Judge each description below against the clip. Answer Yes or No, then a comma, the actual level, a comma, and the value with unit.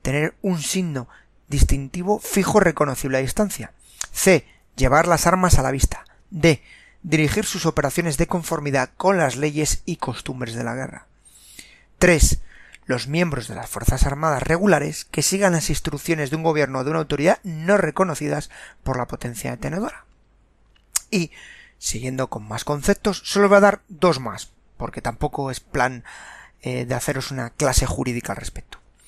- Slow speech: No, average, 160 wpm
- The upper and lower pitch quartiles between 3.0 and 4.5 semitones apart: No, average, 5.3 semitones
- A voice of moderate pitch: Yes, medium, 150 Hz